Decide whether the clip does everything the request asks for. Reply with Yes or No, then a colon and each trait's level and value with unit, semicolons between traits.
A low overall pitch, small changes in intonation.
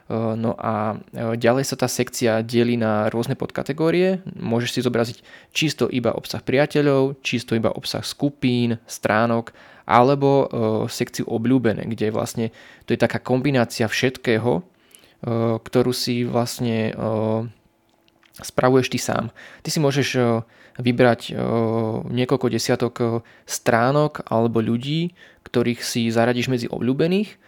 Yes: low, 120 Hz; narrow, 2.3 semitones